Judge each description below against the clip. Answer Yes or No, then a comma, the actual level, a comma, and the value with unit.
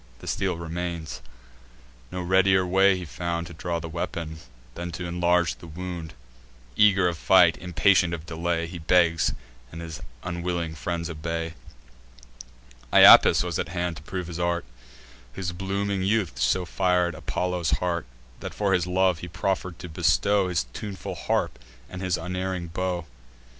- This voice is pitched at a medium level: No, very low, 90 Hz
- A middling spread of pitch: No, narrow, 1.7 semitones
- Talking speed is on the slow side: No, average, 155 wpm